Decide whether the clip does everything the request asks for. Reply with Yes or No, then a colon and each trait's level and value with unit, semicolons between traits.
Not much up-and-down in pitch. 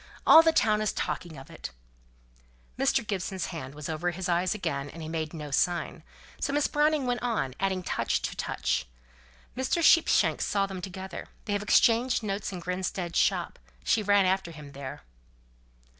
No: average, 4.4 semitones